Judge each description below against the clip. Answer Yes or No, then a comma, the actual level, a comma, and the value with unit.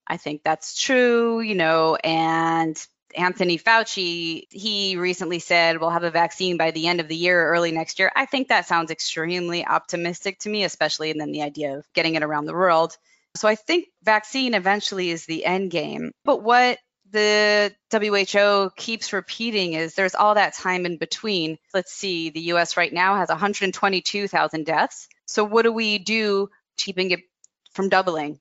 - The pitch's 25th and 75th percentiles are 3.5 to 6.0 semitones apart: Yes, average, 4.0 semitones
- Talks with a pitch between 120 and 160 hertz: No, medium, 185 Hz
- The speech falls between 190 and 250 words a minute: No, average, 175 wpm